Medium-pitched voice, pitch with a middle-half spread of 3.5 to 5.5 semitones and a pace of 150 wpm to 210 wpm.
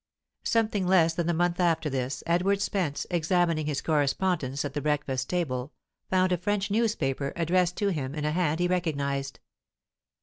Yes: medium, 165 Hz; average, 4.1 semitones; average, 165 wpm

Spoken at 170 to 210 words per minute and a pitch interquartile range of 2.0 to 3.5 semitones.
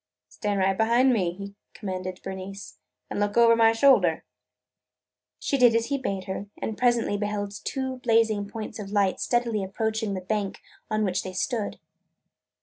No: average, 160 wpm; average, 2.9 semitones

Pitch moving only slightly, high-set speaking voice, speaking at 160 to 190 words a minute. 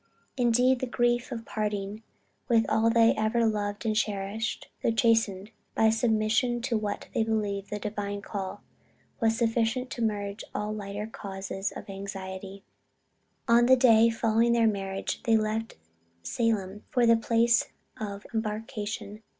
No: narrow, 2.1 semitones; high, 220 Hz; average, 145 wpm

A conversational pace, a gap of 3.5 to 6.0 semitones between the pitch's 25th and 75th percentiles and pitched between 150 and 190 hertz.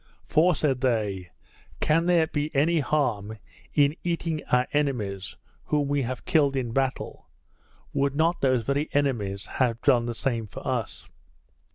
No: average, 150 wpm; average, 4.4 semitones; low, 135 Hz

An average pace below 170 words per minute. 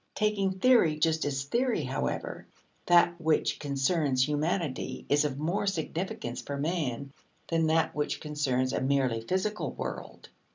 Yes: slow, 135 wpm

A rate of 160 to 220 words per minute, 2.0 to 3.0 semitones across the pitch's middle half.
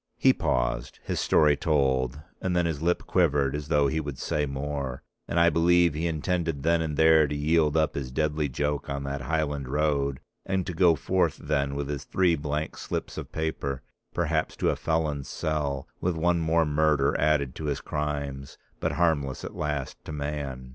Yes: average, 190 wpm; narrow, 2.5 semitones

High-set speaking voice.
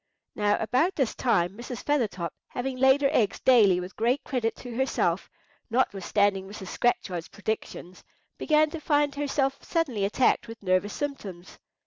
Yes: high, 235 Hz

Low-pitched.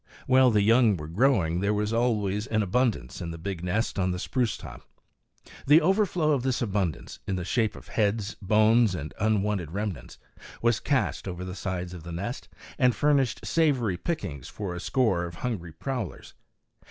Yes: low, 105 Hz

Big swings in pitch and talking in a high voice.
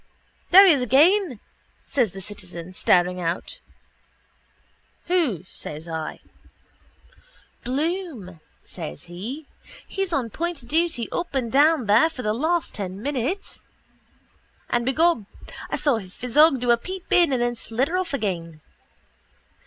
Yes: wide, 8.5 semitones; very high, 250 Hz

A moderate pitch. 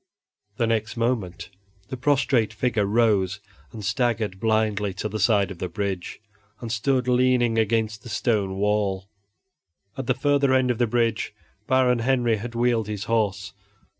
No: low, 115 Hz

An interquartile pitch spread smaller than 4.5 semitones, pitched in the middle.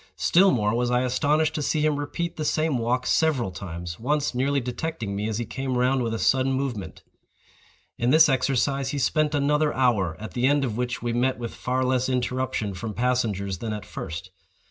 No: average, 3.8 semitones; low, 125 Hz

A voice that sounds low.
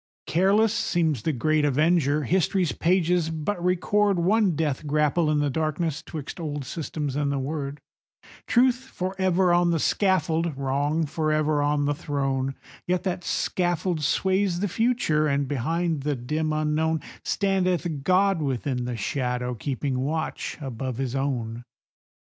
No: medium, 155 Hz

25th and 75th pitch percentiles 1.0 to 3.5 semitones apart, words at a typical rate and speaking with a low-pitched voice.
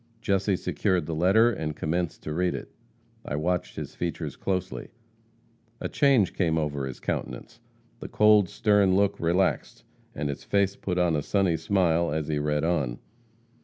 No: average, 4.2 semitones; average, 165 wpm; very low, 85 Hz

